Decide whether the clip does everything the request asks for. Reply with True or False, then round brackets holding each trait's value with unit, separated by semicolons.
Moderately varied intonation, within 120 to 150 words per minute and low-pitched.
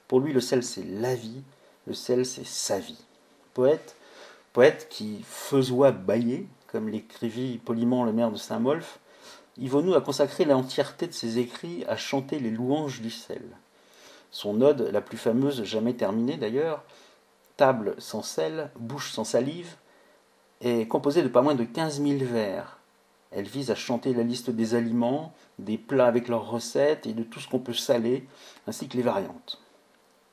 False (3.0 semitones; 165 wpm; 125 Hz)